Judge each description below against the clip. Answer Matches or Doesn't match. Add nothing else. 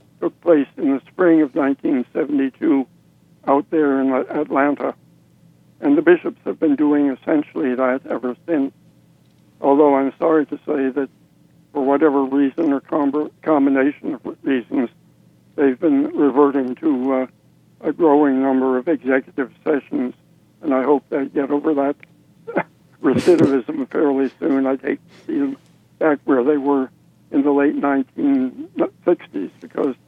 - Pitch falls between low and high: Matches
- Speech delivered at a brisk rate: Doesn't match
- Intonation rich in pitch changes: Doesn't match